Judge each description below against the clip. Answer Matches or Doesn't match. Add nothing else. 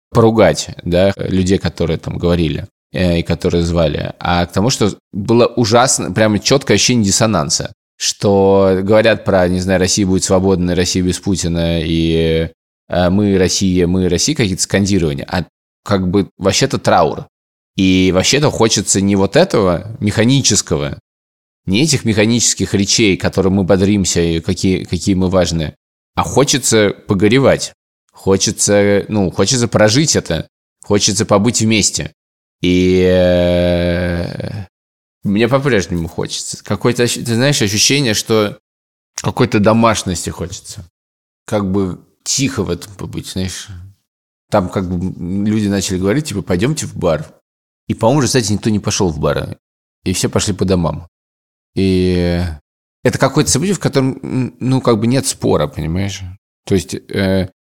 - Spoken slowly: Doesn't match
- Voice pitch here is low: Matches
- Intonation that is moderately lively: Matches